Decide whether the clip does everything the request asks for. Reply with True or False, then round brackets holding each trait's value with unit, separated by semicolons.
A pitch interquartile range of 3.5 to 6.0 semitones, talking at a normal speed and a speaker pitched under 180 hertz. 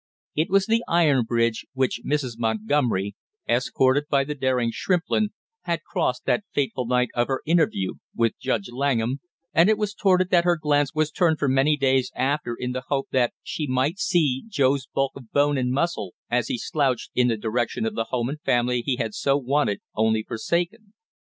True (4.1 semitones; 190 wpm; 135 Hz)